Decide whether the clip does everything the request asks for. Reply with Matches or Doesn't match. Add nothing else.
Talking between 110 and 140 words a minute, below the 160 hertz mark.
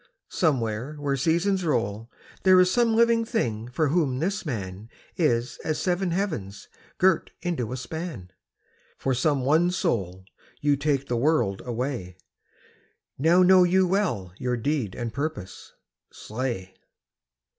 Matches